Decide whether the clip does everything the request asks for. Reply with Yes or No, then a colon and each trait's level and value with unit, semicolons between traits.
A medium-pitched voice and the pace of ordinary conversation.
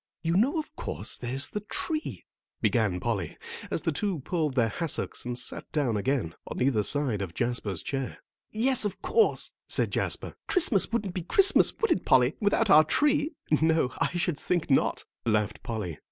Yes: medium, 155 Hz; average, 175 wpm